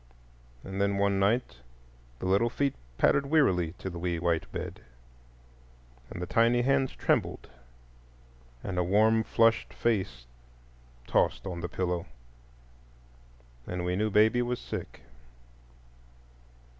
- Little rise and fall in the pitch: No, average, 4.6 semitones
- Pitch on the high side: No, low, 100 Hz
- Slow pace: Yes, slow, 120 wpm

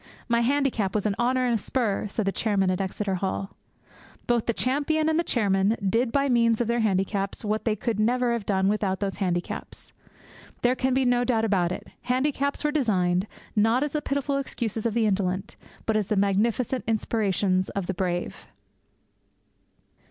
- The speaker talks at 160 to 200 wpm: Yes, average, 180 wpm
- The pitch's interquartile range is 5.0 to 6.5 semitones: No, average, 4.2 semitones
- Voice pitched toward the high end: Yes, high, 220 Hz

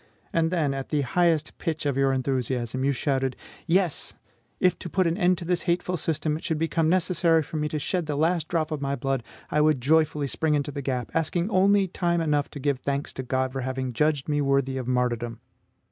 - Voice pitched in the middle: Yes, medium, 150 Hz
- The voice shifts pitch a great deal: No, average, 3.6 semitones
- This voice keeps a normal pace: No, fast, 220 wpm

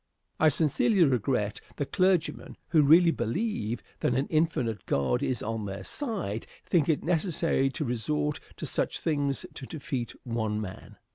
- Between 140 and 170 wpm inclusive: Yes, average, 150 wpm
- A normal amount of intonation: No, wide, 6.3 semitones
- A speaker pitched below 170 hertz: Yes, medium, 140 Hz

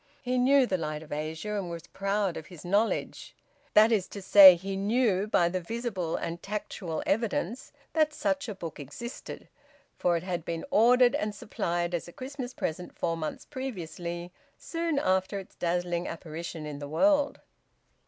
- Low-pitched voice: No, medium, 185 Hz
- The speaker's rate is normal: Yes, average, 165 wpm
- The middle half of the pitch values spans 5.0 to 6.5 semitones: Yes, wide, 5.5 semitones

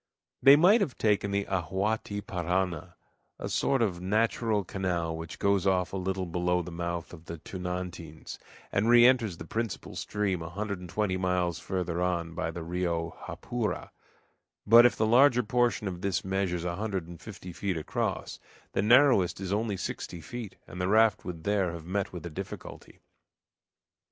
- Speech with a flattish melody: No, average, 3.4 semitones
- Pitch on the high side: No, very low, 95 Hz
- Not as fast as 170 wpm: No, average, 175 wpm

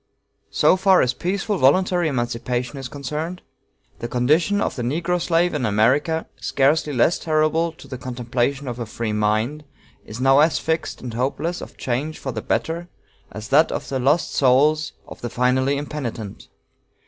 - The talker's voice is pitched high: No, medium, 140 Hz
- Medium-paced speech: Yes, average, 165 wpm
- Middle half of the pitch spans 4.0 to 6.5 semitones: Yes, average, 4.7 semitones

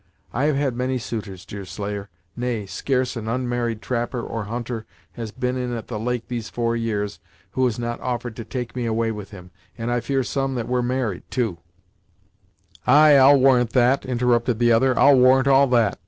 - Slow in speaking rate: No, average, 195 wpm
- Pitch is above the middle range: No, low, 120 Hz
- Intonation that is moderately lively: No, narrow, 2.2 semitones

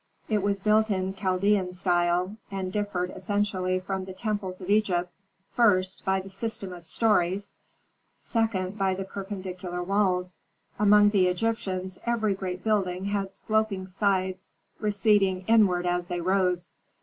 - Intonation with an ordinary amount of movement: No, narrow, 2.1 semitones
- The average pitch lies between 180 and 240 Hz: Yes, high, 190 Hz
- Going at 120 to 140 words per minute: Yes, slow, 135 wpm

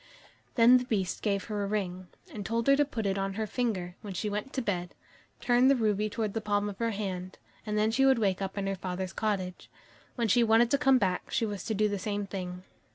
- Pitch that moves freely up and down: No, average, 3.0 semitones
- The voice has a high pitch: Yes, high, 210 Hz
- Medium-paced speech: No, fast, 245 wpm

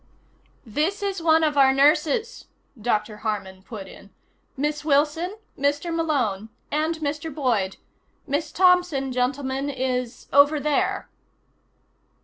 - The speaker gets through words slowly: Yes, slow, 115 wpm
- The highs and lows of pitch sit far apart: No, average, 4.0 semitones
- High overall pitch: Yes, very high, 285 Hz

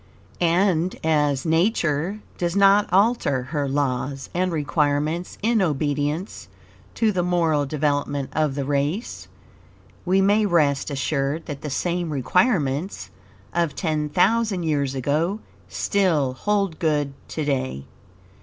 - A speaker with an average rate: No, slow, 120 wpm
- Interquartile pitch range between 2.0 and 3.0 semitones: No, average, 4.3 semitones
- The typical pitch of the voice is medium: Yes, medium, 155 Hz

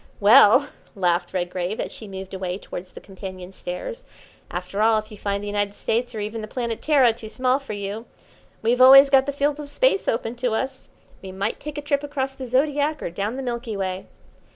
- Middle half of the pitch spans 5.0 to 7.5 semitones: Yes, average, 5.3 semitones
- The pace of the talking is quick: Yes, fast, 210 wpm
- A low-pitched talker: No, high, 225 Hz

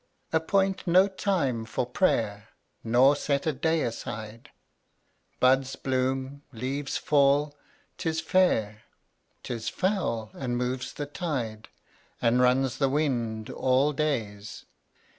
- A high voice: No, low, 130 Hz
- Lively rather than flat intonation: No, average, 4.4 semitones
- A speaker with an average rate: No, slow, 115 wpm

